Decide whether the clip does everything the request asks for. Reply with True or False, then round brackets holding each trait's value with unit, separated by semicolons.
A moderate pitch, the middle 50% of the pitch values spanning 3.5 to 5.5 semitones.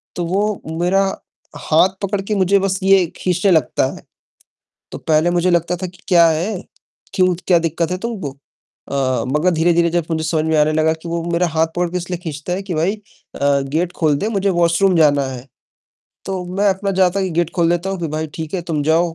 False (175 Hz; 2.9 semitones)